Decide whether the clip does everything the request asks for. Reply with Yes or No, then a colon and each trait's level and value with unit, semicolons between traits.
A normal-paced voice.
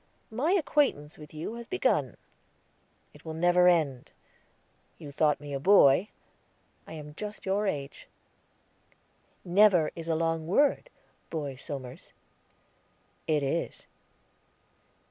No: slow, 115 wpm